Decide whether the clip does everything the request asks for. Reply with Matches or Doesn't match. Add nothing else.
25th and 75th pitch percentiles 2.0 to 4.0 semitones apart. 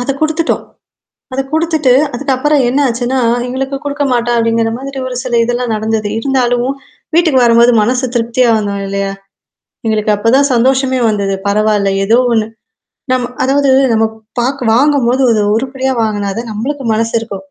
Matches